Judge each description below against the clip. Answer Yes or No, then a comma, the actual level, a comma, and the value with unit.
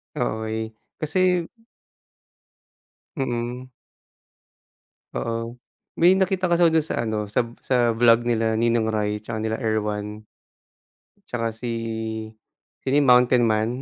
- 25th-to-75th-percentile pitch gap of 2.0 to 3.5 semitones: Yes, narrow, 2.6 semitones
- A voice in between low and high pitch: No, low, 115 Hz